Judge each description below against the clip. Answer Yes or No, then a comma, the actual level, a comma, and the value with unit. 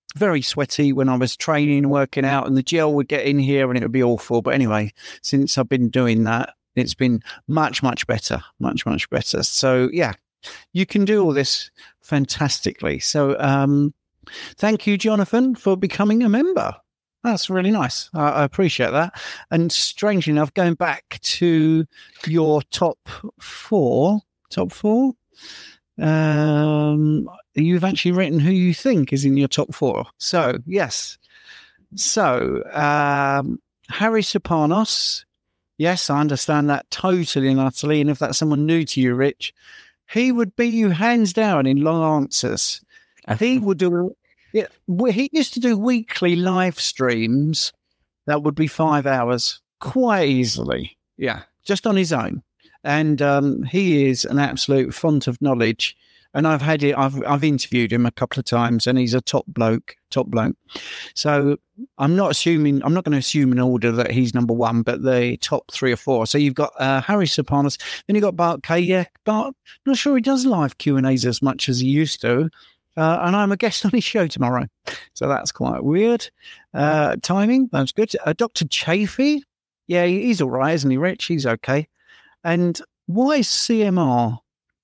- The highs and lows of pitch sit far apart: Yes, wide, 6.3 semitones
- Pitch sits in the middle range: Yes, medium, 155 Hz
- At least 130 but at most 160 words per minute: No, average, 170 wpm